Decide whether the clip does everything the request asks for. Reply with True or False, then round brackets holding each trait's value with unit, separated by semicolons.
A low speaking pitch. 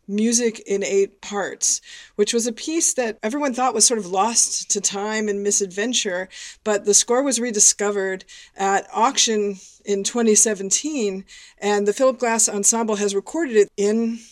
False (215 Hz)